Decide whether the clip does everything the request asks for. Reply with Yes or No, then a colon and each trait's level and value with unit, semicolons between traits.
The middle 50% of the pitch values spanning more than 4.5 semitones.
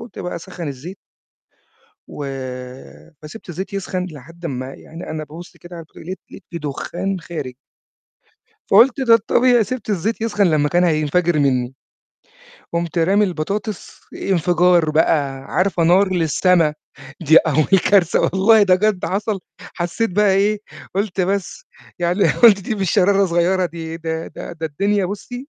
No: average, 3.8 semitones